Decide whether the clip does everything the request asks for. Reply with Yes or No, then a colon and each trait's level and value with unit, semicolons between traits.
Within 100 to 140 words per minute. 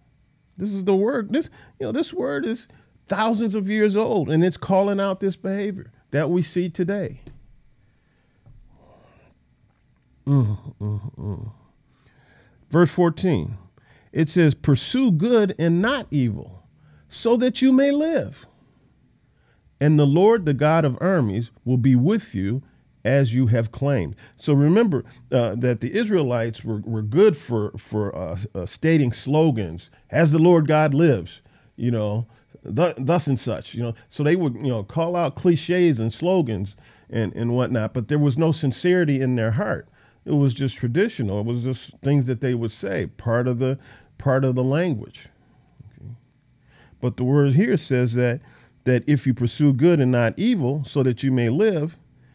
No: average, 165 wpm